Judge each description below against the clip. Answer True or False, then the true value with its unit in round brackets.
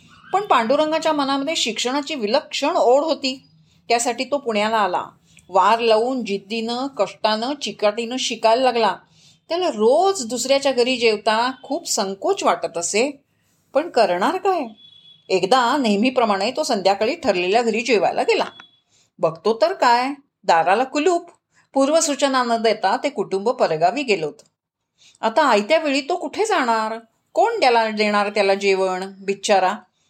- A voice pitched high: True (240 Hz)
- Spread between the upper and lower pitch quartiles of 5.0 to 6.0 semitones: True (5.5 semitones)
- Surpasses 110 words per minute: True (125 wpm)